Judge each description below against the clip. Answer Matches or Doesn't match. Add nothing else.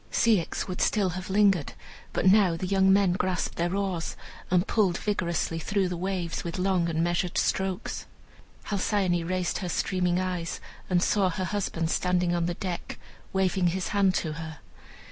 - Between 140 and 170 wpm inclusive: Matches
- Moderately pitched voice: Matches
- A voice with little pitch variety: Matches